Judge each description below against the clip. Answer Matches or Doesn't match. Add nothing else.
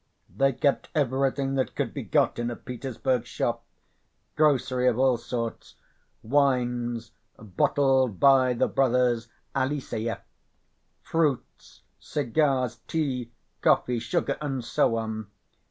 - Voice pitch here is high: Doesn't match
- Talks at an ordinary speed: Doesn't match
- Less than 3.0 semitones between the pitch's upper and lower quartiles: Matches